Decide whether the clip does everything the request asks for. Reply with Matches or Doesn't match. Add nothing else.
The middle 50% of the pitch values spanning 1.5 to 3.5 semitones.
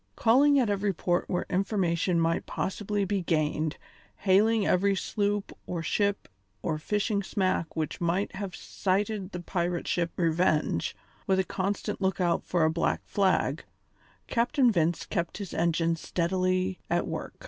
Matches